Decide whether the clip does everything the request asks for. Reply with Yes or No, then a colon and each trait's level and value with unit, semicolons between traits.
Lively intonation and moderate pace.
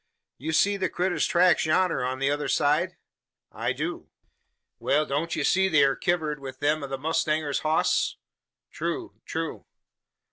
No: average, 3.5 semitones; average, 150 wpm